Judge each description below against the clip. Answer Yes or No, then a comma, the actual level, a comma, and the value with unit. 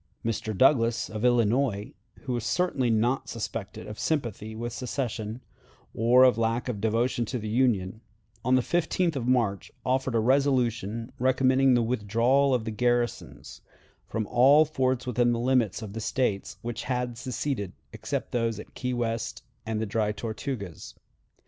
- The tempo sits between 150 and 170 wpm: Yes, average, 155 wpm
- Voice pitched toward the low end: Yes, low, 120 Hz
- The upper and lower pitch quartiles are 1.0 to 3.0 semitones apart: Yes, average, 2.7 semitones